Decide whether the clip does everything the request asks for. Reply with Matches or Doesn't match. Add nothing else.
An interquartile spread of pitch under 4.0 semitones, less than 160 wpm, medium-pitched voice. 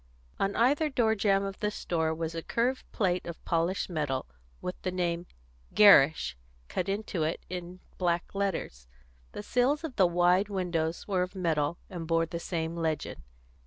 Doesn't match